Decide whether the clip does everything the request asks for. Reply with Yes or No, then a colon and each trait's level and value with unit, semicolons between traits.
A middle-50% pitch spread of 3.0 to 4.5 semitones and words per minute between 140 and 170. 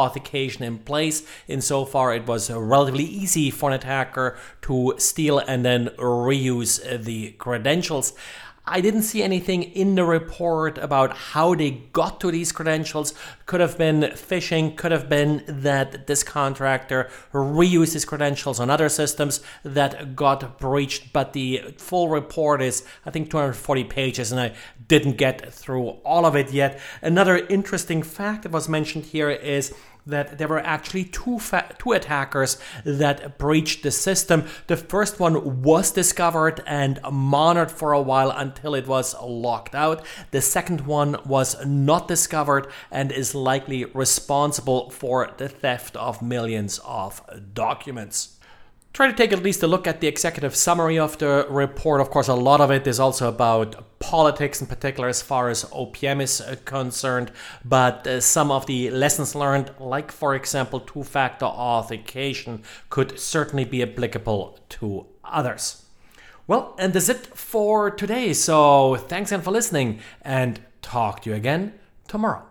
Yes: average, 3.4 semitones; average, 155 wpm